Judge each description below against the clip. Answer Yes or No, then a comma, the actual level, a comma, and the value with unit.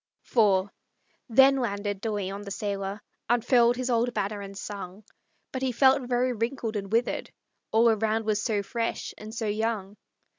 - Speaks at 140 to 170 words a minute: Yes, average, 160 wpm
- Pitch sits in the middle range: No, high, 220 Hz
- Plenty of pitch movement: No, average, 2.8 semitones